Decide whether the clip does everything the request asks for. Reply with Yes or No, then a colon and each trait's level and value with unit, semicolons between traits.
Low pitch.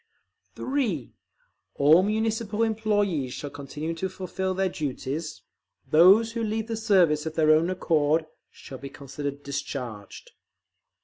No: medium, 165 Hz